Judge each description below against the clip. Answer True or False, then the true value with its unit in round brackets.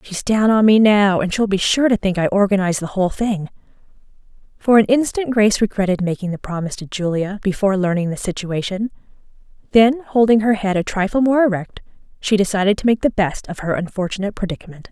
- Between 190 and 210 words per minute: True (195 wpm)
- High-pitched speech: True (200 Hz)